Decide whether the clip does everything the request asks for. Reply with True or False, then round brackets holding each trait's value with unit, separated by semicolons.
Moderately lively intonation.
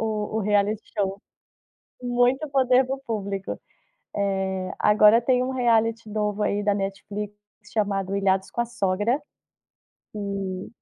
True (3.1 semitones)